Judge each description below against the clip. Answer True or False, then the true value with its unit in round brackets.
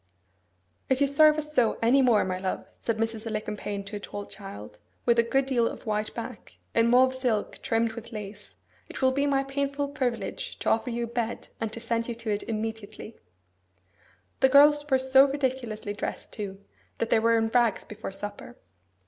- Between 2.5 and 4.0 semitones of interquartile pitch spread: True (3.6 semitones)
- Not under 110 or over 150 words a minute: False (190 wpm)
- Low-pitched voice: False (230 Hz)